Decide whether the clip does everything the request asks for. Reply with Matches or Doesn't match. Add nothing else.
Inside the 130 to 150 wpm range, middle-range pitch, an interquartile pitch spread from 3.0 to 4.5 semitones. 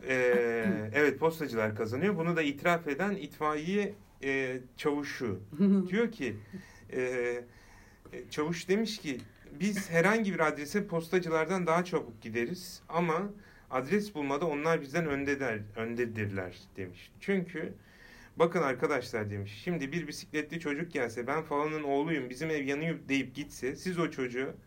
Doesn't match